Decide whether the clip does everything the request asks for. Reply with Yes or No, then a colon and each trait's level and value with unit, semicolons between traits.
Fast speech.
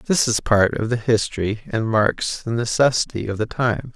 No: average, 195 wpm